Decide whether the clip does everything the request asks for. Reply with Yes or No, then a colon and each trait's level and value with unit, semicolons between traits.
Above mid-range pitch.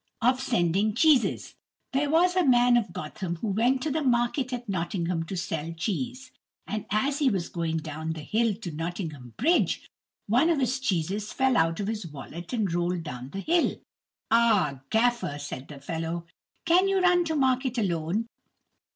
Yes: high, 215 Hz